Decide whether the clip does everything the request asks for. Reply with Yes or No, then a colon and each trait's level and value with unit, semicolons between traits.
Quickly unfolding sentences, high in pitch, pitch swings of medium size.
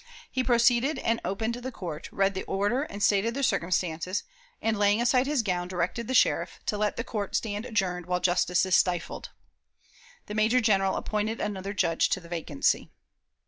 No: average, 180 wpm; high, 205 Hz; average, 4.2 semitones